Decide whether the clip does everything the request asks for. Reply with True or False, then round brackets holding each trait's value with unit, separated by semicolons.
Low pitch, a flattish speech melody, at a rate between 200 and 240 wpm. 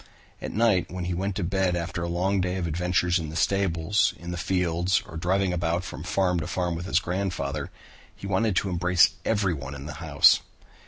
True (90 Hz; 2.0 semitones; 205 wpm)